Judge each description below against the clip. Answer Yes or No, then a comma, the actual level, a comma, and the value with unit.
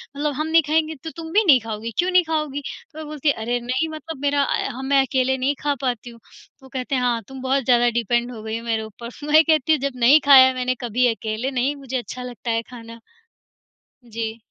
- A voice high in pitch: Yes, very high, 260 Hz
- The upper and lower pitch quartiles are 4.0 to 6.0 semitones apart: No, average, 3.6 semitones